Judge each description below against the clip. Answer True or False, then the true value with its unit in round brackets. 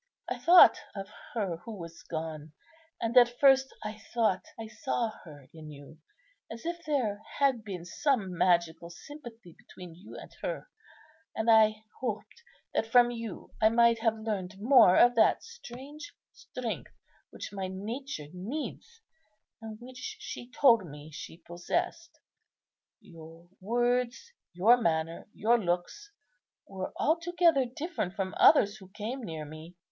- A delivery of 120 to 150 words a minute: True (140 wpm)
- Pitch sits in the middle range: False (220 Hz)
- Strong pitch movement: True (5.9 semitones)